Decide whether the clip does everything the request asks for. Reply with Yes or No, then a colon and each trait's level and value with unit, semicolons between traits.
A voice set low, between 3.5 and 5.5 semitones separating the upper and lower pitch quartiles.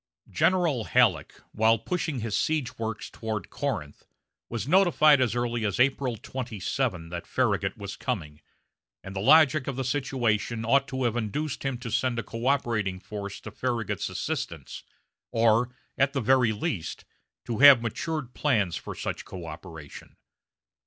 Yes: low, 120 Hz; average, 4.3 semitones